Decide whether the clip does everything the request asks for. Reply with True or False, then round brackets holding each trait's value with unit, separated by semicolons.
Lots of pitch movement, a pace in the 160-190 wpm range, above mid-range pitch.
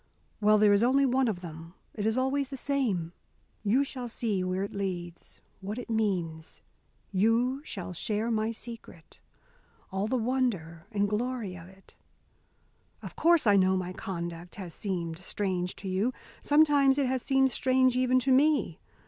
True (5.7 semitones; 165 wpm; 215 Hz)